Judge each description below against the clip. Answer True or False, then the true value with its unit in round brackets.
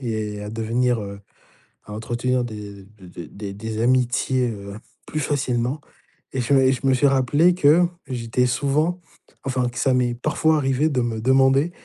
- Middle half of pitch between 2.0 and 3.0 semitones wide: False (3.4 semitones)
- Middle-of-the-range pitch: False (125 Hz)